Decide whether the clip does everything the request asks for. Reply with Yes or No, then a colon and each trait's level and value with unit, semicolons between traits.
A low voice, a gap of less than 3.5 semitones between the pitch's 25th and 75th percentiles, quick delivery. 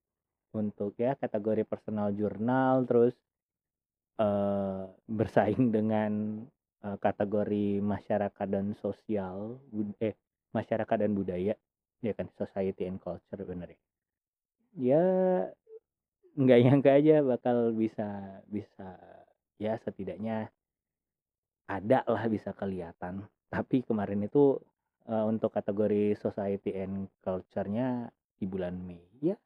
No: low, 105 Hz; average, 2.8 semitones; average, 105 wpm